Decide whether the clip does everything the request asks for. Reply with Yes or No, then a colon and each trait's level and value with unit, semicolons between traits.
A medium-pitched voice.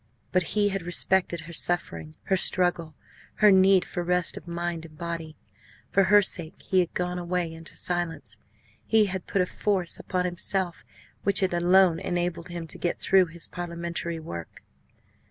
Yes: medium, 175 Hz